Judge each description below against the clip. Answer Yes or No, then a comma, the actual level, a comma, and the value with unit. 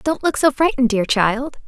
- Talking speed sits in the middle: No, fast, 215 wpm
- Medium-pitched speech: No, very high, 260 Hz